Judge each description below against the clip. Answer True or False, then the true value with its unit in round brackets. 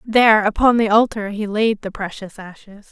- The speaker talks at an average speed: True (185 wpm)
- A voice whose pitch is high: True (210 Hz)